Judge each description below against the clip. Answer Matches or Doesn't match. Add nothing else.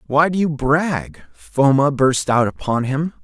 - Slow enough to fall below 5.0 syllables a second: Matches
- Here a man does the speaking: Matches